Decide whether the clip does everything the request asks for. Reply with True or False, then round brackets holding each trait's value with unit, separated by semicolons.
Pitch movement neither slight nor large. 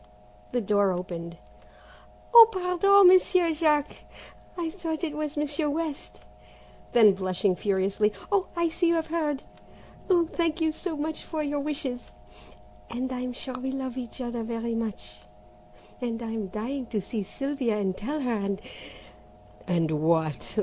False (7.8 semitones)